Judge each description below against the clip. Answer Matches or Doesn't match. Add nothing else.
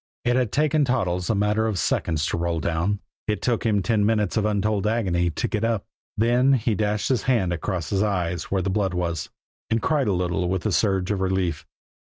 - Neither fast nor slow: Doesn't match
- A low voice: Matches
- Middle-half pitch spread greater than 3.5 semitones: Matches